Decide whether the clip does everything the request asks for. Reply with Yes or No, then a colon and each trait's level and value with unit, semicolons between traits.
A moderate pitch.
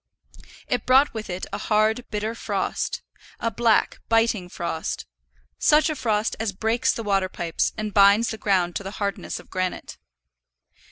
No: high, 215 Hz